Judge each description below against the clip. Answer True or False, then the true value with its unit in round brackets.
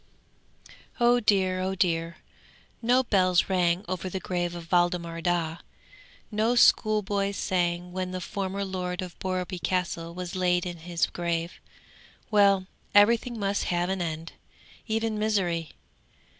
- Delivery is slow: True (130 wpm)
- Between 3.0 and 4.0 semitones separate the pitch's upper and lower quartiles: False (2.4 semitones)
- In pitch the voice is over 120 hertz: True (185 Hz)